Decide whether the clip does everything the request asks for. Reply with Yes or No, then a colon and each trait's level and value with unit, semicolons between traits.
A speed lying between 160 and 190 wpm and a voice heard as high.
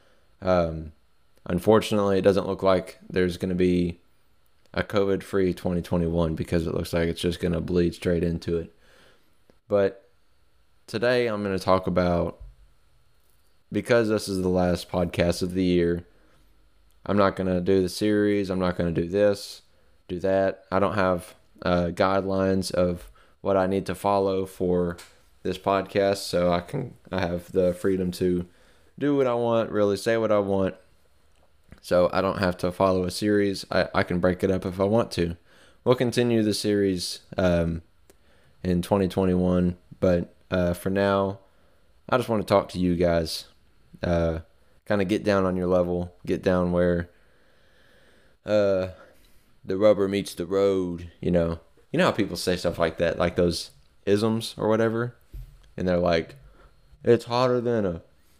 No: average, 170 wpm; very low, 90 Hz